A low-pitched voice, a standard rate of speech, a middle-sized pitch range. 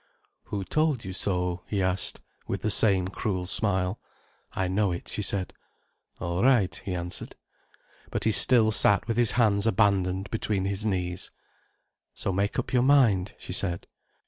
Yes: low, 100 Hz; average, 160 wpm; average, 3.0 semitones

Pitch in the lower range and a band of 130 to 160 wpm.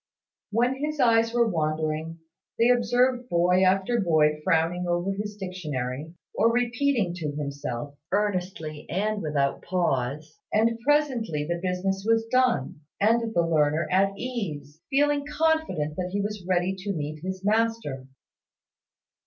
No: medium, 185 Hz; slow, 135 wpm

